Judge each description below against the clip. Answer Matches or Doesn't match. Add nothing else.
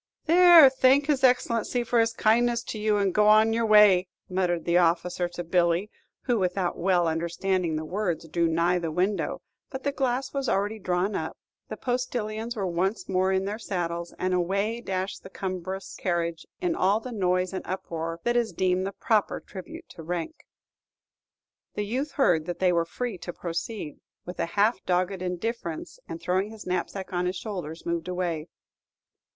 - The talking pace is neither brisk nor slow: Matches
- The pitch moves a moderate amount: Matches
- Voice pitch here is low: Doesn't match